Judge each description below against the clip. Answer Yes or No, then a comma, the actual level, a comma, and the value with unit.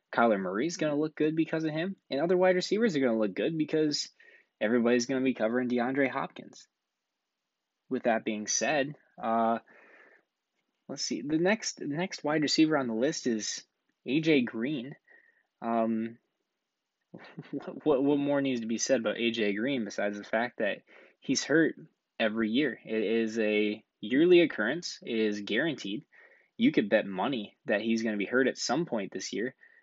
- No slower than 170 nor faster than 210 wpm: Yes, average, 175 wpm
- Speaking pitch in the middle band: No, low, 130 Hz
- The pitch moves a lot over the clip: Yes, wide, 5.7 semitones